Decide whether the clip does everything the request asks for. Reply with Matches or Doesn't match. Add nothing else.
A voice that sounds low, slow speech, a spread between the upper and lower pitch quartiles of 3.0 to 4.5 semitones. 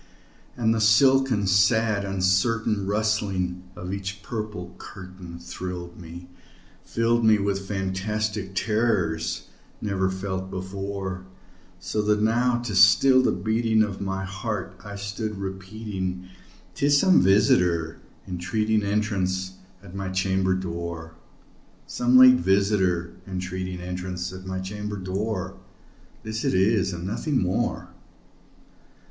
Doesn't match